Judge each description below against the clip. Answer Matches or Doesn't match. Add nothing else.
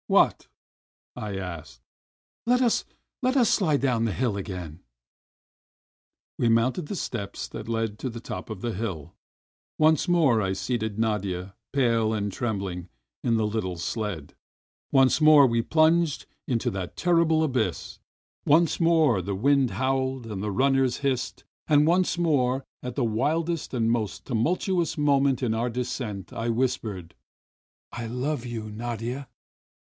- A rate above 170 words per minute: Doesn't match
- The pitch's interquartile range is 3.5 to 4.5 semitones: Doesn't match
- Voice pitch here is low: Matches